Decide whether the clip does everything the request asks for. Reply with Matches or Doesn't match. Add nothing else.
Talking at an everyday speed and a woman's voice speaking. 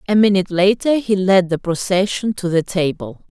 Matches